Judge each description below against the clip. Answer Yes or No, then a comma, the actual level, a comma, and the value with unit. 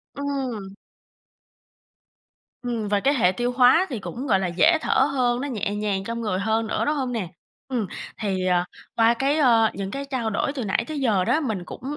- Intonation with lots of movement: No, average, 4.9 semitones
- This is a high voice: Yes, high, 230 Hz